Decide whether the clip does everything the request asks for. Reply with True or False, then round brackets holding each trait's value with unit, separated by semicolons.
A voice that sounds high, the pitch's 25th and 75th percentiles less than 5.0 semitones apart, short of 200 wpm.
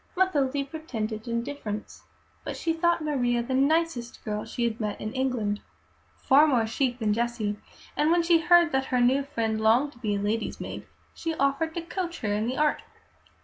False (260 Hz; 5.6 semitones; 190 wpm)